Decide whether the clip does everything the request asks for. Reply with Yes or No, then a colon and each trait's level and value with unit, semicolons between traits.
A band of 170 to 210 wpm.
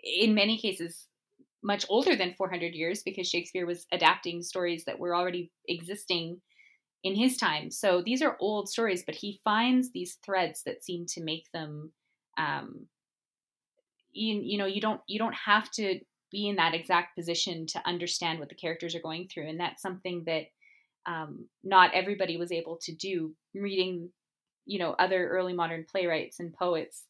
Yes: average, 175 wpm